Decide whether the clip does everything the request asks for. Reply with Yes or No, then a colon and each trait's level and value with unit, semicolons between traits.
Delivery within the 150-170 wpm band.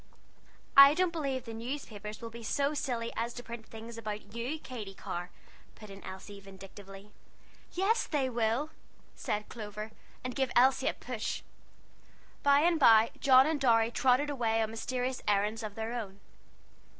Yes: average, 160 wpm